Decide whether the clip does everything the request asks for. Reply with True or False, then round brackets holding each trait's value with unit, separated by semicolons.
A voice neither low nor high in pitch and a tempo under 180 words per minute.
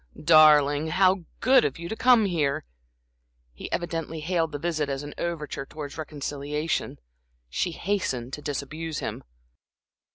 True (155 Hz; 135 wpm)